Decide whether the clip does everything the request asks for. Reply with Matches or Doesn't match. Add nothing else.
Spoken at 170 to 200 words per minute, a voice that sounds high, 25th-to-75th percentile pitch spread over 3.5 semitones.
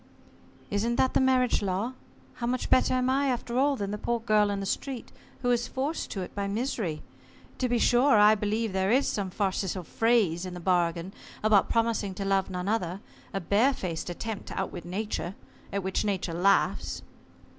Matches